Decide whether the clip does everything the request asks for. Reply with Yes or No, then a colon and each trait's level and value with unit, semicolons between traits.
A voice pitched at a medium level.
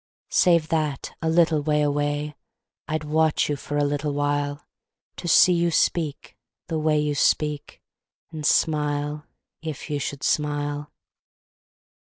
Yes: medium, 150 Hz